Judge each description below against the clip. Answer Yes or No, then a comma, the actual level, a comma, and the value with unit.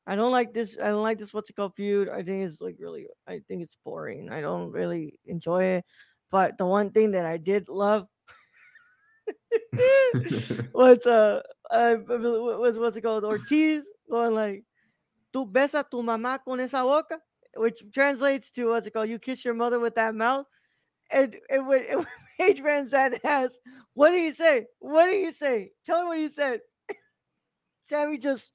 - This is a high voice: Yes, high, 245 Hz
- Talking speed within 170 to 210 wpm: Yes, average, 180 wpm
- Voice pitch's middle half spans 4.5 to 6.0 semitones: Yes, wide, 5.5 semitones